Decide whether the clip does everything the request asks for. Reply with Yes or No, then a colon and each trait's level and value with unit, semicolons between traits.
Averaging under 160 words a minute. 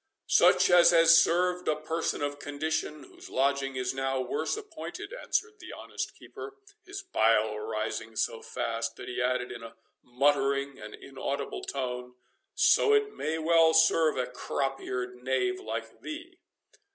Yes: average, 150 wpm